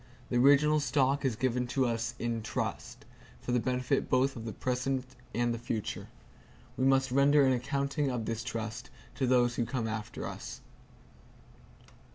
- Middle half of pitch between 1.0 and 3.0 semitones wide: Yes, narrow, 2.6 semitones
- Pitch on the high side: No, low, 125 Hz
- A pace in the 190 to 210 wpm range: No, average, 165 wpm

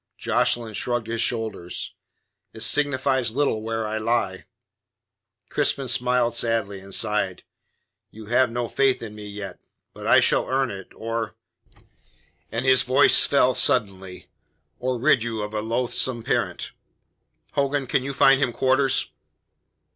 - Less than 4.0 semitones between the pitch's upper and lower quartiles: Yes, average, 3.2 semitones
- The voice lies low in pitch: Yes, low, 115 Hz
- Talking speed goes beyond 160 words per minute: No, average, 140 wpm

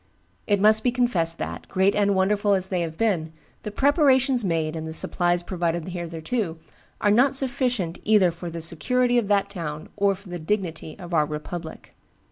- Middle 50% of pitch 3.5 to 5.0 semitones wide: Yes, average, 4.5 semitones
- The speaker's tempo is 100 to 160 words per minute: No, average, 180 wpm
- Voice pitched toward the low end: No, high, 190 Hz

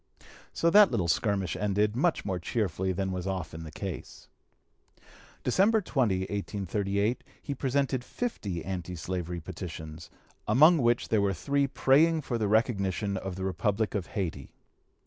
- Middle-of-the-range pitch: No, low, 100 Hz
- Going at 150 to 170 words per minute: No, average, 140 wpm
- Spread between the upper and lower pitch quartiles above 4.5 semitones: Yes, average, 5.2 semitones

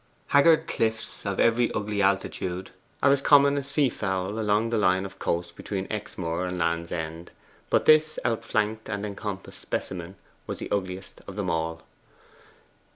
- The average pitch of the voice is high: No, low, 100 Hz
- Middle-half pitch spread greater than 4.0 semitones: No, average, 3.7 semitones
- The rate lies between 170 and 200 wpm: No, average, 155 wpm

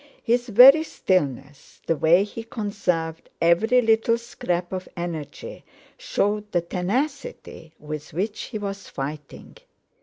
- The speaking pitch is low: No, high, 190 Hz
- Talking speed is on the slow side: Yes, slow, 120 wpm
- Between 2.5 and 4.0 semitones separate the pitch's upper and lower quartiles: No, wide, 5.5 semitones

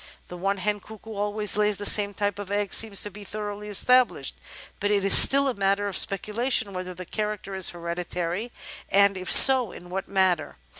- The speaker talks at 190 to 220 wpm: Yes, average, 195 wpm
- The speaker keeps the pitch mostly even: Yes, narrow, 1.8 semitones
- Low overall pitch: No, high, 205 Hz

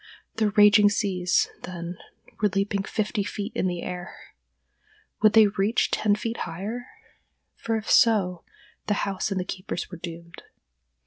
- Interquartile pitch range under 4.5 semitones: Yes, average, 2.9 semitones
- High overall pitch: Yes, high, 200 Hz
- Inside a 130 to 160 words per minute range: Yes, average, 140 wpm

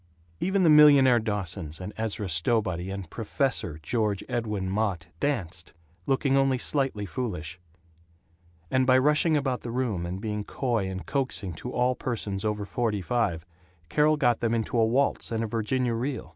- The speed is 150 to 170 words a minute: Yes, average, 160 wpm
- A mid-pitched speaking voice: No, low, 115 Hz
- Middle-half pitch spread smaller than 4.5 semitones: No, average, 5.0 semitones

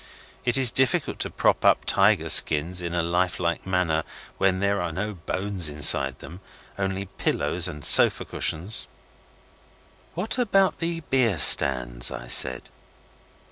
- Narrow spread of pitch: No, average, 4.8 semitones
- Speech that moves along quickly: No, average, 140 wpm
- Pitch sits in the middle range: No, very low, 90 Hz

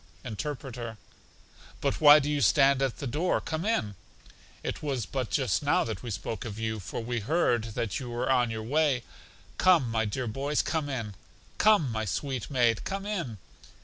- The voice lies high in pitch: No, low, 125 Hz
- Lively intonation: No, average, 4.6 semitones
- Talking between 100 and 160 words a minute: No, average, 180 wpm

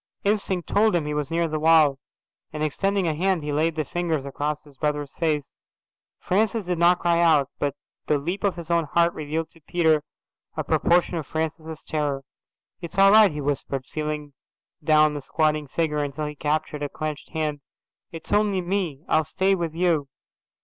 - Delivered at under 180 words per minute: No, average, 185 wpm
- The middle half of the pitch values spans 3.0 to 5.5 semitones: No, narrow, 2.6 semitones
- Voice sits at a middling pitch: Yes, medium, 155 Hz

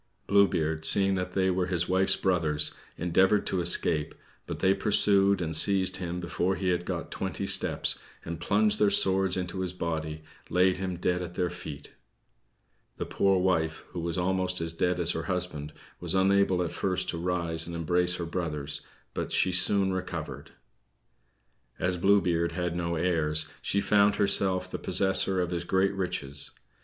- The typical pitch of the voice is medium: No, very low, 90 Hz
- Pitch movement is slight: Yes, narrow, 2.1 semitones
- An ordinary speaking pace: Yes, average, 170 wpm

